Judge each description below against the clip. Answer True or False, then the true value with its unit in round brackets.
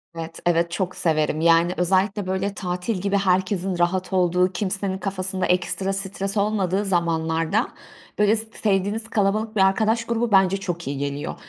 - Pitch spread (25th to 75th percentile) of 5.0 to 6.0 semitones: False (2.5 semitones)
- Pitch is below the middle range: False (190 Hz)